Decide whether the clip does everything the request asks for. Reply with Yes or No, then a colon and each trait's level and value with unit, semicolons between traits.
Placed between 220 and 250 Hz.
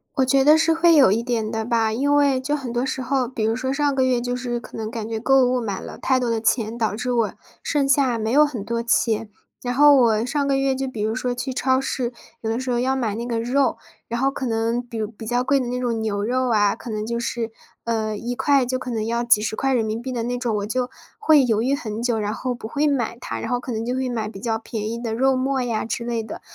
Yes: high, 240 Hz